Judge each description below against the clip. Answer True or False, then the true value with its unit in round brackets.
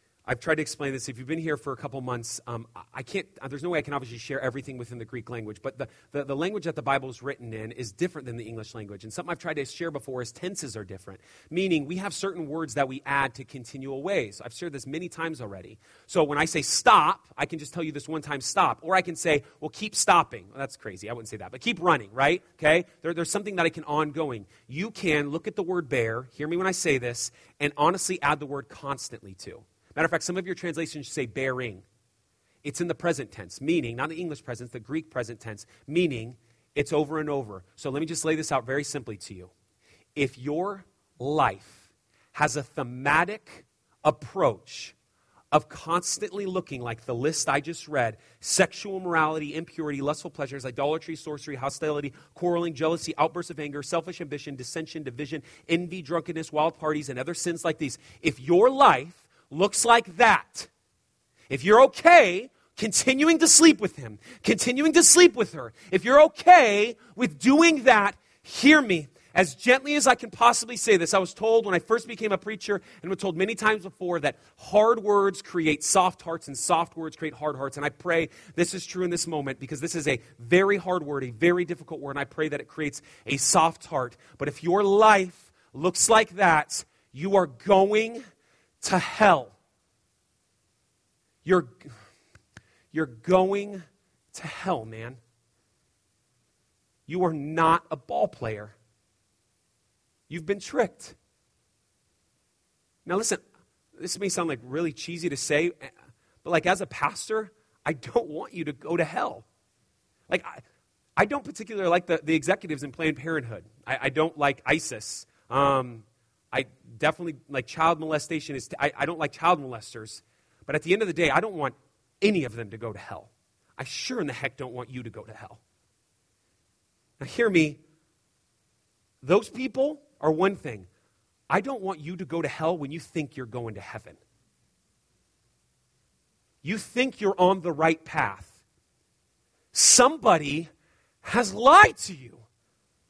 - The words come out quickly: False (190 wpm)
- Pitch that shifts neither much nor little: False (5.7 semitones)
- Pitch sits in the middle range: True (155 Hz)